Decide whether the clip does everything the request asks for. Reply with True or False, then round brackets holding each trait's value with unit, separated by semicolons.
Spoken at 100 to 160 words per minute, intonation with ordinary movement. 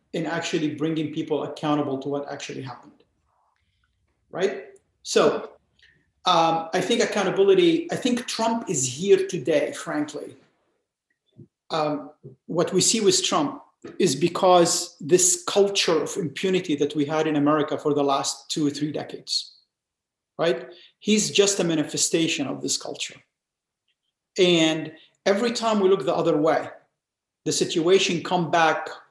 True (135 wpm; 4.3 semitones)